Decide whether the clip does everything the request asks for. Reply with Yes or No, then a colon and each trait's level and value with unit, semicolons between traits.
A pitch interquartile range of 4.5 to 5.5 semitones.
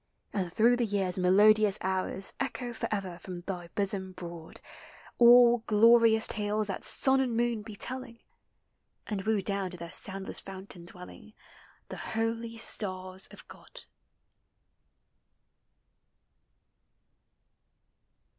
No: average, 3.5 semitones